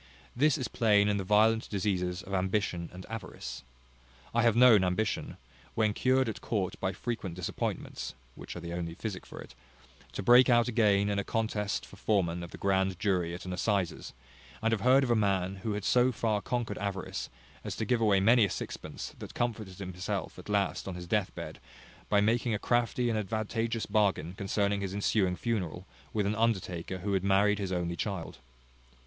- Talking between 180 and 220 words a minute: Yes, average, 190 wpm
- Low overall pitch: Yes, low, 100 Hz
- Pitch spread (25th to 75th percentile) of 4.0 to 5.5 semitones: No, average, 3.2 semitones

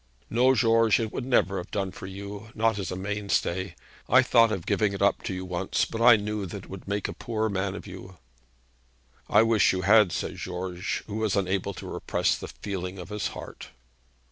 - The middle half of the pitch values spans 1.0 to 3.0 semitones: Yes, average, 2.7 semitones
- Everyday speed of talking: No, fast, 210 wpm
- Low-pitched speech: Yes, low, 100 Hz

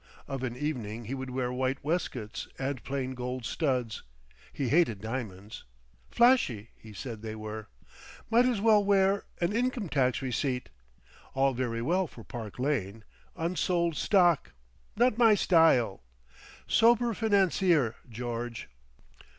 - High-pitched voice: No, low, 135 Hz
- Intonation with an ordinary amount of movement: No, wide, 7.6 semitones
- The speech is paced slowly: Yes, slow, 125 wpm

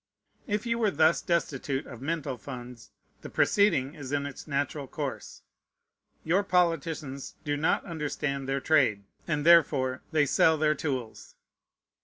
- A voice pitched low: No, medium, 145 Hz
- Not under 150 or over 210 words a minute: No, average, 140 wpm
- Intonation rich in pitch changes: No, average, 3.5 semitones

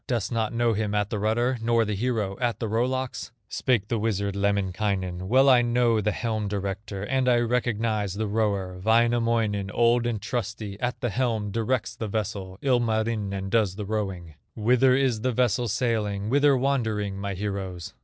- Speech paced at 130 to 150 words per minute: No, average, 175 wpm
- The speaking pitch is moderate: No, low, 110 Hz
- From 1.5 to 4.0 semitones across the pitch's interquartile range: Yes, average, 3.0 semitones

